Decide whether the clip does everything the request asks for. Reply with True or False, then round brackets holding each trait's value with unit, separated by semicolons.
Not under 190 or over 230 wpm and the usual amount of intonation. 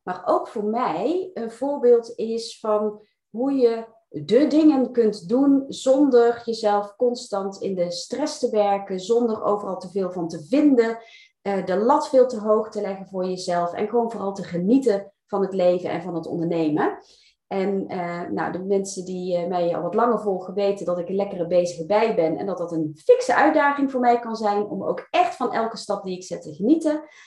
True (195 wpm; 5.0 semitones)